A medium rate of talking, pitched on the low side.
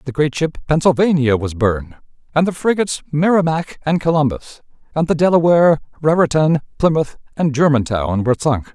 No: average, 145 wpm; medium, 150 Hz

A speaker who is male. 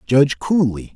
Yes: male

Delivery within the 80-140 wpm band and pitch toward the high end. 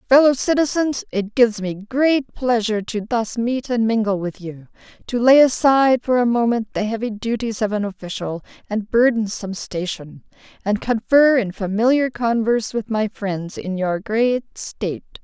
No: average, 160 wpm; high, 225 Hz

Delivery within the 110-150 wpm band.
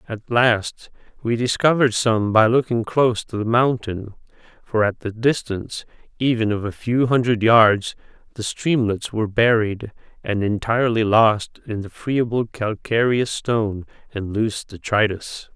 Yes: average, 140 wpm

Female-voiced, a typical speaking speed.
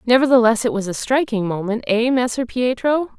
Yes: female; average, 170 wpm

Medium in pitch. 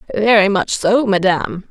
No: high, 200 Hz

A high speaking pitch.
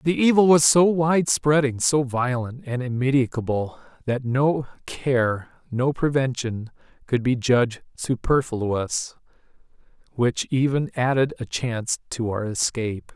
No: low, 130 Hz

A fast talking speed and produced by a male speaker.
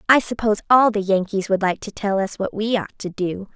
No: fast, 255 wpm; female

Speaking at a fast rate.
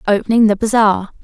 No: average, 145 wpm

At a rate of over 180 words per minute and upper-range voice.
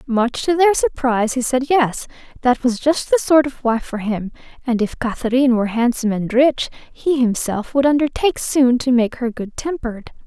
Yes: average, 195 wpm; very high, 255 Hz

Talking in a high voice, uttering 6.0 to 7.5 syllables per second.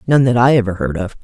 No: low, 115 Hz; 6.7 syllables/s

